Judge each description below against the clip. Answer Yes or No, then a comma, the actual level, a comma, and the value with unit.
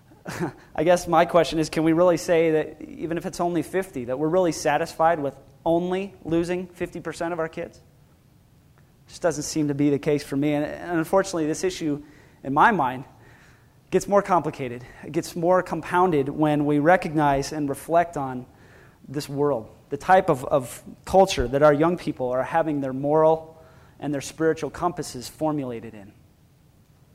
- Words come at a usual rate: Yes, average, 170 wpm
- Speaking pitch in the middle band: Yes, medium, 155 Hz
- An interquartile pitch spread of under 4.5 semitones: Yes, average, 3.4 semitones